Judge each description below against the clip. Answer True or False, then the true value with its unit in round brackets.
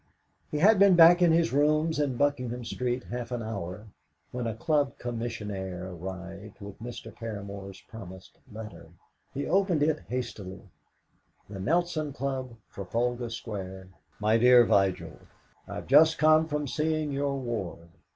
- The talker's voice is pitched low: True (120 Hz)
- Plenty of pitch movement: True (6.6 semitones)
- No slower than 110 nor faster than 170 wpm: True (140 wpm)